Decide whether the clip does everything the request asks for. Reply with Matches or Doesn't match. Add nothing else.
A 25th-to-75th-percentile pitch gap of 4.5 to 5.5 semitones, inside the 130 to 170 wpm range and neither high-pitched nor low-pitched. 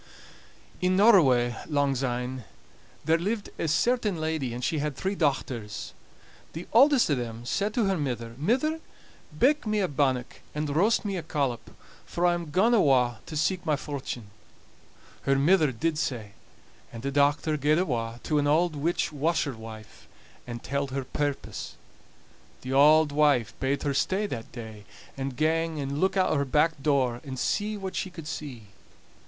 Matches